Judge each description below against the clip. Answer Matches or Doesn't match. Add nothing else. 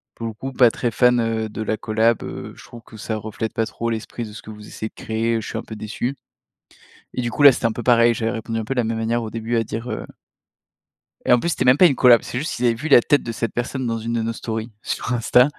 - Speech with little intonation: Matches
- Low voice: Matches